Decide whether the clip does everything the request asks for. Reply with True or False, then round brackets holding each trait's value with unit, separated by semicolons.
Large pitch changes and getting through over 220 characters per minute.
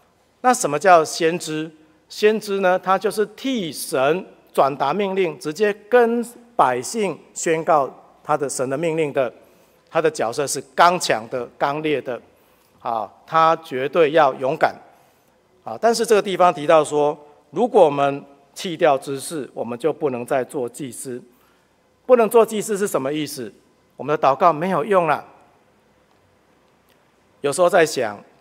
False (5.9 semitones; 215 characters per minute)